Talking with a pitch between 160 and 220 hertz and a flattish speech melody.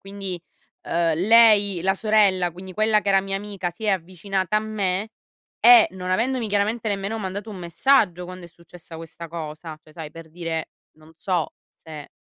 No: high, 190 Hz; average, 3.6 semitones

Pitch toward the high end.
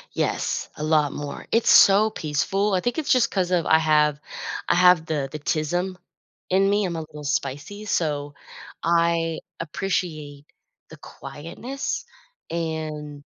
No: medium, 165 Hz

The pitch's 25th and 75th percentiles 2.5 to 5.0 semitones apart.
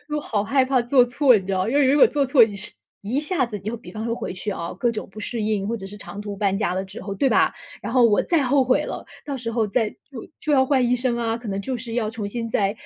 Yes: average, 3.9 semitones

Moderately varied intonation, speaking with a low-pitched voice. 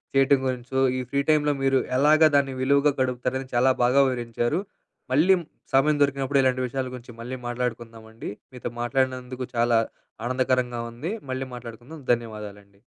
No: narrow, 2.2 semitones; low, 130 Hz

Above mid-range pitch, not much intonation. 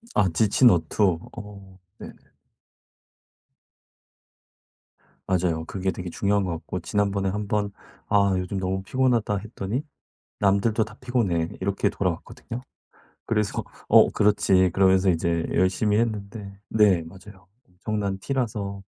No: low, 100 Hz; narrow, 2.2 semitones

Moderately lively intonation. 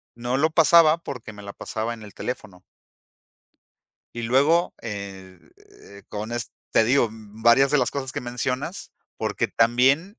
Yes: average, 4.4 semitones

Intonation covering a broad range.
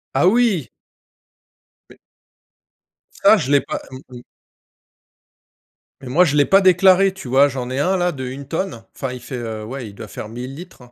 Yes: wide, 6.3 semitones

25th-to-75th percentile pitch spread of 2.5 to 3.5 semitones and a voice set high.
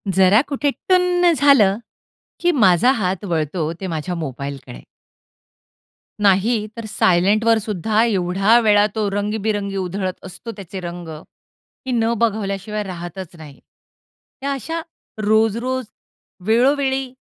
No: average, 4.3 semitones; high, 205 Hz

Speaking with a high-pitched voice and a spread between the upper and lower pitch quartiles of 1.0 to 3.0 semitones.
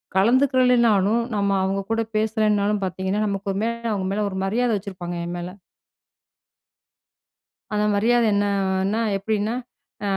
Yes: high, 205 Hz; narrow, 2.6 semitones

